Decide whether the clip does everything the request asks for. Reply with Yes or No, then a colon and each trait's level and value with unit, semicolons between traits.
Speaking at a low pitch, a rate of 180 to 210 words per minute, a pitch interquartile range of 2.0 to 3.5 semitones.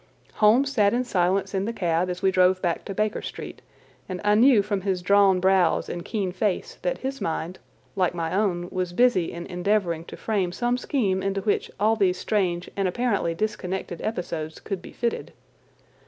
No: high, 190 Hz; average, 185 wpm; average, 3.0 semitones